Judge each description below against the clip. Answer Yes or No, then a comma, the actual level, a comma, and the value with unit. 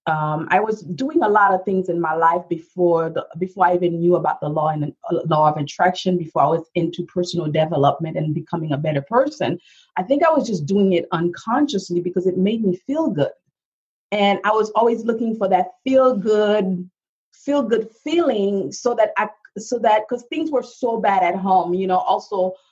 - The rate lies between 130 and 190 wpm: No, fast, 205 wpm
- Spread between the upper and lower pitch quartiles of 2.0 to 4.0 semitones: No, average, 4.6 semitones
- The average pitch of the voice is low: No, medium, 185 Hz